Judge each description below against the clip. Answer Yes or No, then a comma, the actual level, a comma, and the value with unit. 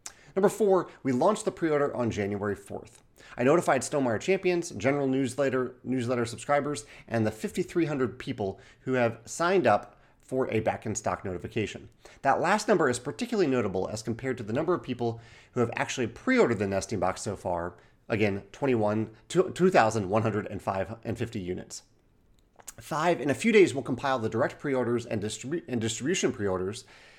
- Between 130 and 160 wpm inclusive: Yes, average, 155 wpm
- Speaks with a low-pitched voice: Yes, low, 120 Hz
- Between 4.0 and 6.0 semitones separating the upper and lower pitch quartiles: Yes, average, 4.8 semitones